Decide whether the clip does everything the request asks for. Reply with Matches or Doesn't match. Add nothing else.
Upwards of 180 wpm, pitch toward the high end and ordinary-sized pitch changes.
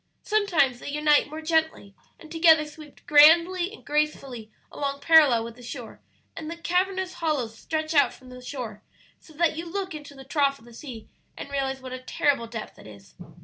Matches